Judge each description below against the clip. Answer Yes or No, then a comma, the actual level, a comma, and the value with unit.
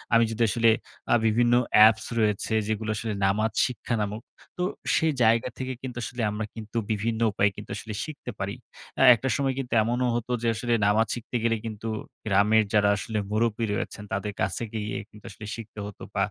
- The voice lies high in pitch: No, low, 110 Hz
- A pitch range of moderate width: No, narrow, 2.0 semitones